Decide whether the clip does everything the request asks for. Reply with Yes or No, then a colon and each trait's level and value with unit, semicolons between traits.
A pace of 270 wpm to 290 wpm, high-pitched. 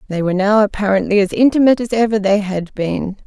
No: average, 200 wpm; high, 205 Hz